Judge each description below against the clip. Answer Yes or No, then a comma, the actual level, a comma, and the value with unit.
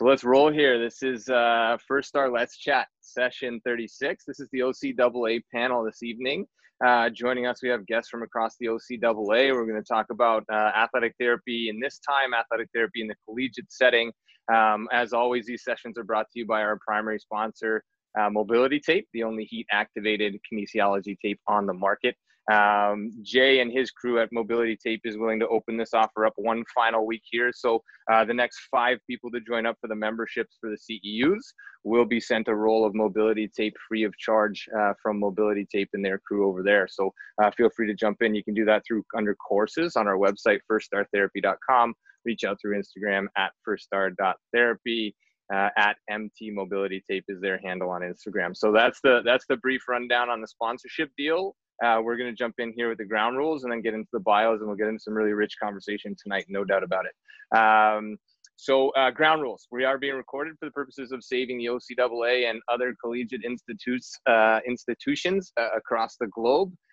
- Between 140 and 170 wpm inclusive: No, fast, 205 wpm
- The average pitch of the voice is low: Yes, low, 115 Hz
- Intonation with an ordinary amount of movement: No, narrow, 2.3 semitones